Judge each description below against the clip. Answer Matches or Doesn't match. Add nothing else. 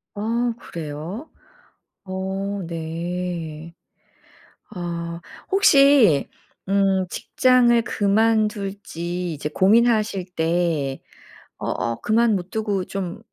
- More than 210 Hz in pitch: Doesn't match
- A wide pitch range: Doesn't match